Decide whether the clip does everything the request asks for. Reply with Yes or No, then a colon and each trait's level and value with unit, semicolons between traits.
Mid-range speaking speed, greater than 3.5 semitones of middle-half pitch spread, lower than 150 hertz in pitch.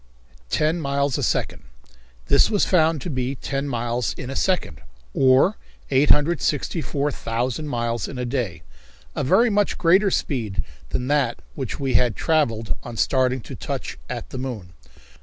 Yes: average, 155 wpm; average, 4.1 semitones; low, 135 Hz